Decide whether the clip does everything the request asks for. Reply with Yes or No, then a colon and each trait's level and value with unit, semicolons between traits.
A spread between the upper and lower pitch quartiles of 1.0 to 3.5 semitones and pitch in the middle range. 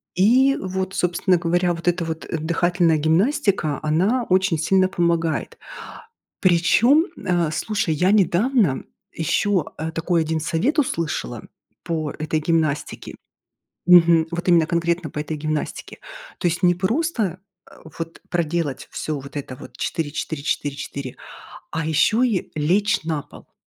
Yes: average, 3.0 semitones; medium, 170 Hz